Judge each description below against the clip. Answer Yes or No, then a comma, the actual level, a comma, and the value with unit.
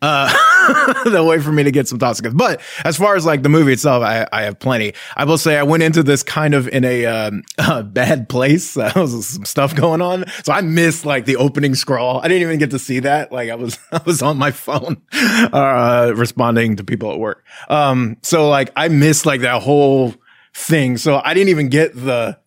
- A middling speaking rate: No, fast, 225 wpm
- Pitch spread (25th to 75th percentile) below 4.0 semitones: No, average, 4.3 semitones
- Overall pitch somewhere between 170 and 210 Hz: No, medium, 140 Hz